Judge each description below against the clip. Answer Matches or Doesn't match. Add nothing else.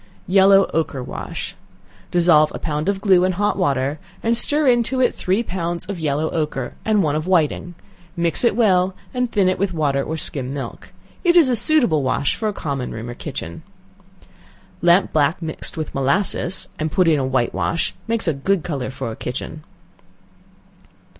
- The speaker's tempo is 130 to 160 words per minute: Doesn't match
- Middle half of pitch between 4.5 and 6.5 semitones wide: Matches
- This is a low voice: Doesn't match